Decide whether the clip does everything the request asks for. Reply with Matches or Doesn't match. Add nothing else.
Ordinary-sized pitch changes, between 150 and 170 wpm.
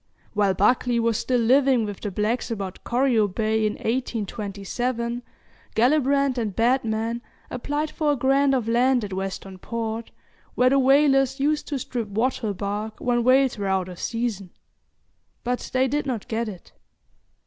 Matches